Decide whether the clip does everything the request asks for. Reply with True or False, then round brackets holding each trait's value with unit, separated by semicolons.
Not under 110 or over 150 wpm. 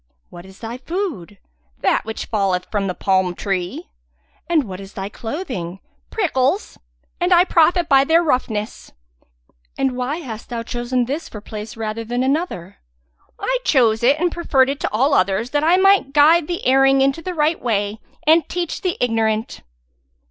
False (170 wpm)